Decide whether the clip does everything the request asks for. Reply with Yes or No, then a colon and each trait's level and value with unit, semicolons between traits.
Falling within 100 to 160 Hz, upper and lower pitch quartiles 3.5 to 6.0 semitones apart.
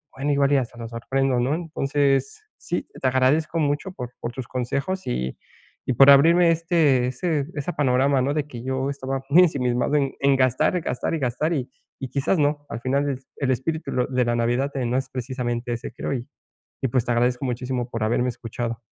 No: low, 135 Hz; average, 2.8 semitones